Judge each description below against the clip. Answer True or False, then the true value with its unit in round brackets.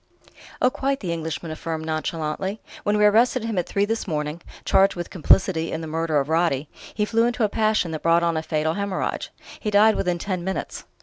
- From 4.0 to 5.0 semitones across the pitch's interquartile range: True (4.6 semitones)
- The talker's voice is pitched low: False (175 Hz)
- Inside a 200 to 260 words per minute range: True (205 wpm)